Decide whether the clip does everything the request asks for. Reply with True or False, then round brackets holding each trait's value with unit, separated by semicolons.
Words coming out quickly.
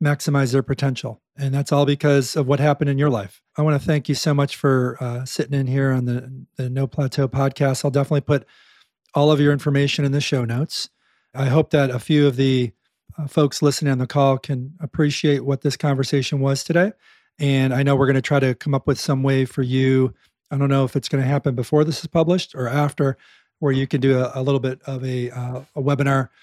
True (235 wpm)